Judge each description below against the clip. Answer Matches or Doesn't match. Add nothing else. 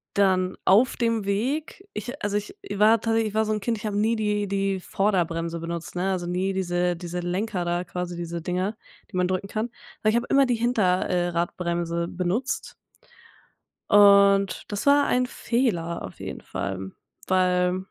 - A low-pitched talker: Doesn't match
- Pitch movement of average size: Matches